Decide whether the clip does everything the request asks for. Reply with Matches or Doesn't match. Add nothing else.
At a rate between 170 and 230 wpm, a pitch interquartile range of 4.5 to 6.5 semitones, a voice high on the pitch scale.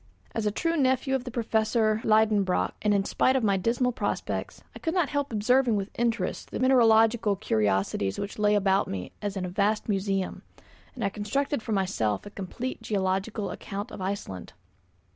Doesn't match